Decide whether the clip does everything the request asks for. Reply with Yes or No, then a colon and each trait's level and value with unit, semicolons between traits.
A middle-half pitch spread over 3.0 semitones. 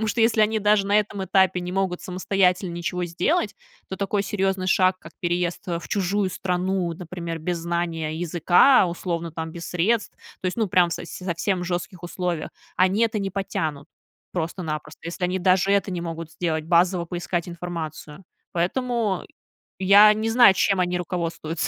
No: narrow, 2.4 semitones